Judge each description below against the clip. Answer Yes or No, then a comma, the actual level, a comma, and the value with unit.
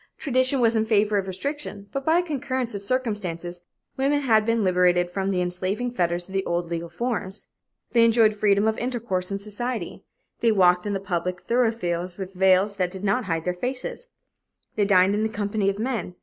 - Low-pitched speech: No, high, 205 Hz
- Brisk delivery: No, average, 195 wpm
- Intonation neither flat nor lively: Yes, average, 4.4 semitones